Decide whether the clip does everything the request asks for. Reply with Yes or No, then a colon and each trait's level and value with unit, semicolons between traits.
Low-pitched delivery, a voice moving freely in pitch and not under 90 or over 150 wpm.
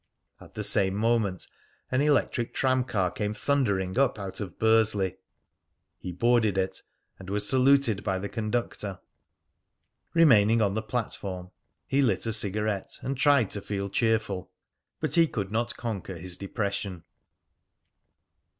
No: low, 105 Hz; average, 3.8 semitones; average, 140 wpm